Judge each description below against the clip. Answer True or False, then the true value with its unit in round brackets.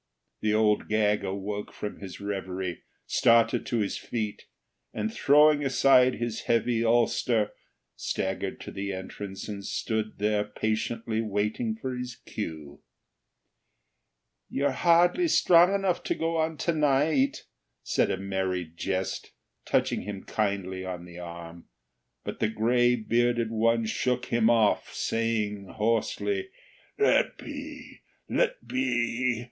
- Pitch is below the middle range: True (110 Hz)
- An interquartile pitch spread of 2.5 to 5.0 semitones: True (3.9 semitones)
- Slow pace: True (125 wpm)